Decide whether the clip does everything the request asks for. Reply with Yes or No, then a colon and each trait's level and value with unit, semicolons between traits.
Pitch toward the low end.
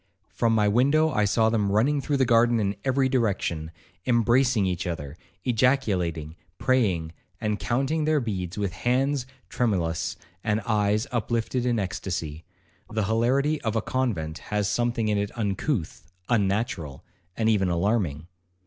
Yes: low, 110 Hz